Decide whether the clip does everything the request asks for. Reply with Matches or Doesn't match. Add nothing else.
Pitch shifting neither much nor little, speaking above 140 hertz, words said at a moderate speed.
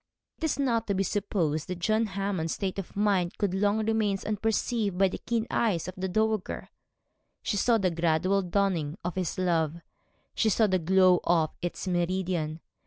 Matches